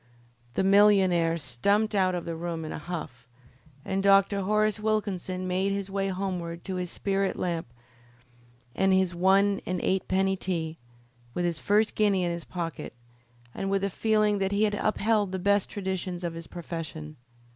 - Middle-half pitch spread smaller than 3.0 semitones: Yes, narrow, 2.5 semitones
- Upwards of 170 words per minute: No, average, 165 wpm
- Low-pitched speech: No, high, 190 Hz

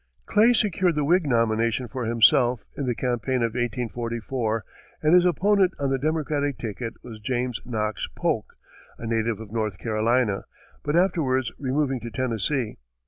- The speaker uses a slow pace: No, average, 150 wpm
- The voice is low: Yes, low, 125 Hz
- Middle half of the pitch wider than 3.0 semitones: Yes, average, 4.1 semitones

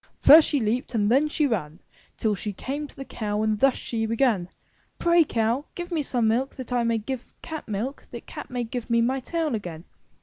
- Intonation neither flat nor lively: Yes, average, 3.9 semitones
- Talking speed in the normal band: No, fast, 225 wpm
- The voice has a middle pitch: No, high, 240 Hz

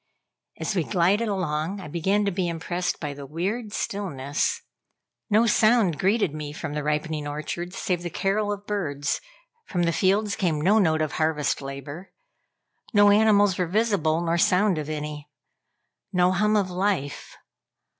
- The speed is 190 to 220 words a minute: No, average, 155 wpm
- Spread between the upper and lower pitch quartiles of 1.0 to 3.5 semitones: No, average, 4.9 semitones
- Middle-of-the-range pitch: Yes, medium, 175 Hz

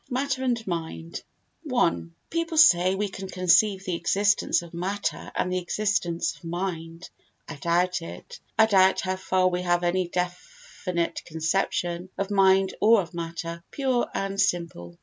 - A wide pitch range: No, average, 2.9 semitones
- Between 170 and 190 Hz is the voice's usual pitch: Yes, medium, 185 Hz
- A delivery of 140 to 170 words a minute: Yes, average, 150 wpm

